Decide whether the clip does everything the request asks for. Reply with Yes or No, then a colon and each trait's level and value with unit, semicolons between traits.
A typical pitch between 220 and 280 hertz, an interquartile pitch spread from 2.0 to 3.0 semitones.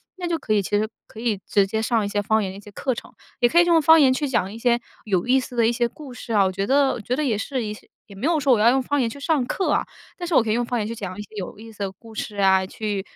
No: high, 230 Hz; average, 4.4 semitones